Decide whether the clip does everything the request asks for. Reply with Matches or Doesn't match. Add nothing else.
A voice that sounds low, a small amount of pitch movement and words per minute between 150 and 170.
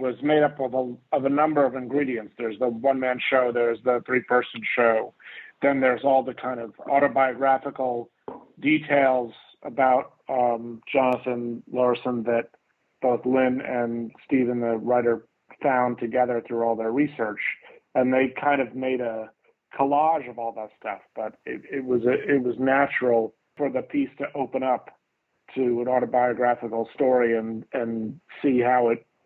Matches